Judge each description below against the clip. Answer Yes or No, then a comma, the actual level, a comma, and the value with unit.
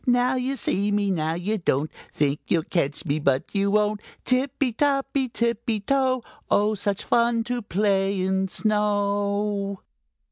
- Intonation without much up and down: No, average, 3.7 semitones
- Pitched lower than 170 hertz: No, high, 205 Hz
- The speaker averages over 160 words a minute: No, average, 145 wpm